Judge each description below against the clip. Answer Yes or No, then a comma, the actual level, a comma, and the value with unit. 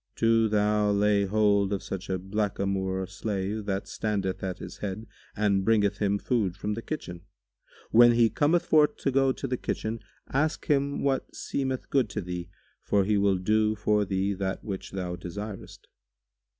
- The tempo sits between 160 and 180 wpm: Yes, average, 170 wpm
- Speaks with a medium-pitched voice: No, low, 105 Hz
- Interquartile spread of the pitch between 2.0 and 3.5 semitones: Yes, average, 2.8 semitones